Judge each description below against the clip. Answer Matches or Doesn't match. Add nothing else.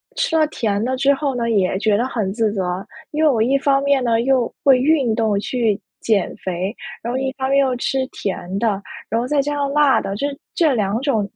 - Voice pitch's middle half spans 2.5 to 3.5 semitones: Doesn't match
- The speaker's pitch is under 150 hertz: Doesn't match